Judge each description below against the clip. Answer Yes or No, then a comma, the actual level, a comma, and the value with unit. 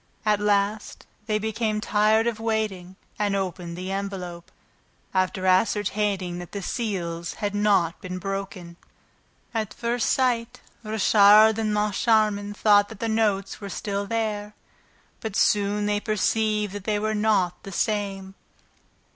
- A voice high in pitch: Yes, high, 205 Hz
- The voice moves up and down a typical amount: No, narrow, 1.9 semitones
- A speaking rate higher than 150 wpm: No, slow, 135 wpm